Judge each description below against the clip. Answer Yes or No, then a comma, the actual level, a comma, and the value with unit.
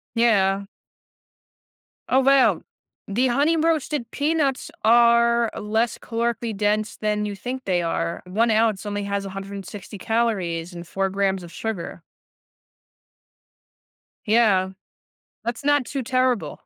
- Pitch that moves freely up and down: No, average, 3.4 semitones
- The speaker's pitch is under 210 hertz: No, high, 220 Hz